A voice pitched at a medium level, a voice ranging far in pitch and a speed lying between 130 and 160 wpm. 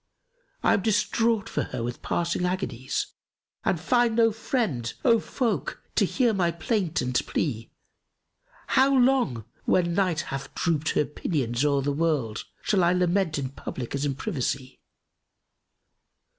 Yes: medium, 170 Hz; wide, 7.9 semitones; average, 150 wpm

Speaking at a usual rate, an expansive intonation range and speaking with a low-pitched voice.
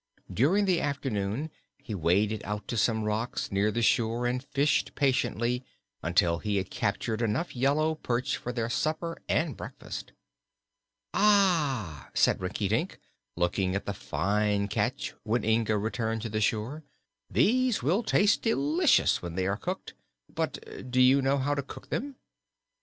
Yes: average, 150 wpm; wide, 6.0 semitones; low, 120 Hz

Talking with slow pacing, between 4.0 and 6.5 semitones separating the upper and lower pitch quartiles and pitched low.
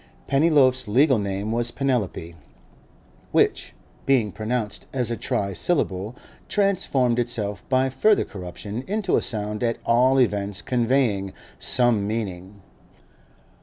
Yes: slow, 110 wpm; average, 4.4 semitones; low, 115 Hz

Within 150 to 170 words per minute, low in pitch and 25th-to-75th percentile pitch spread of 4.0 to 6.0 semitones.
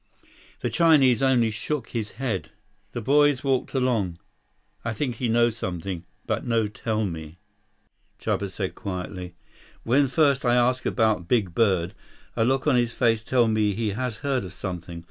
Yes: average, 165 wpm; low, 115 Hz; average, 4.6 semitones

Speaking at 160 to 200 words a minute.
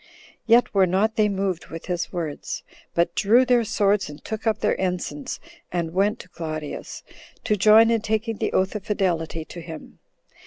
Yes: average, 180 wpm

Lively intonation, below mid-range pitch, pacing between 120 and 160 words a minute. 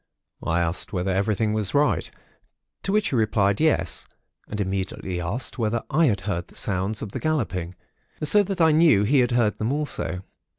No: wide, 7.0 semitones; low, 110 Hz; average, 185 wpm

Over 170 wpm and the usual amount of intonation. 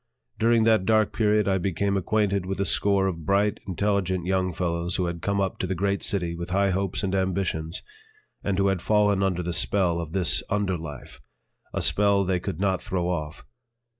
No: average, 195 wpm; narrow, 2.2 semitones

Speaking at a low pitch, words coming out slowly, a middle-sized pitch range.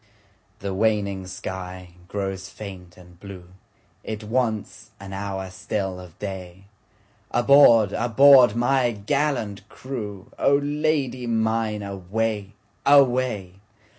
Yes: low, 105 Hz; slow, 90 wpm; average, 3.9 semitones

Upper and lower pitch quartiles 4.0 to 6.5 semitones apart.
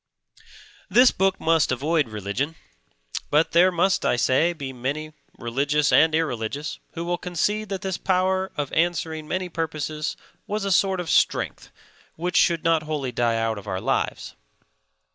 Yes: average, 4.3 semitones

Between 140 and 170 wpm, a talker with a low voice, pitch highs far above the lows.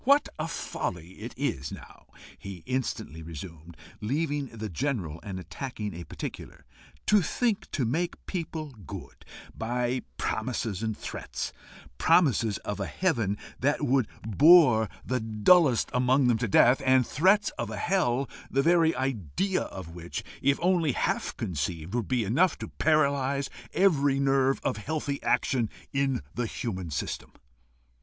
Yes: average, 145 wpm; low, 125 Hz; wide, 5.8 semitones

